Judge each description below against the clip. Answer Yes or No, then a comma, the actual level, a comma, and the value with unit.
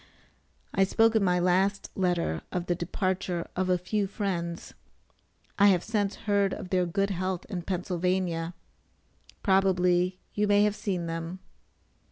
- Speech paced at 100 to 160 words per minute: Yes, average, 145 wpm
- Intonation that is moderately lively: No, narrow, 1.9 semitones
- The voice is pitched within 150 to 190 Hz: Yes, medium, 185 Hz